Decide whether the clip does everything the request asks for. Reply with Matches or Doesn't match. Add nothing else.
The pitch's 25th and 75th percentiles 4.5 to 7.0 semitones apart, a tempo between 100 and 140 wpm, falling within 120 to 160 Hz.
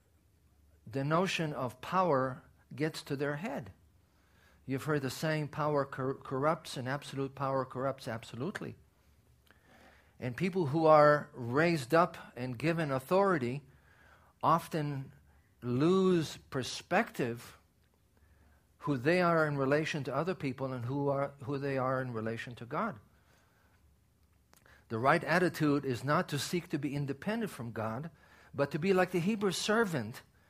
Matches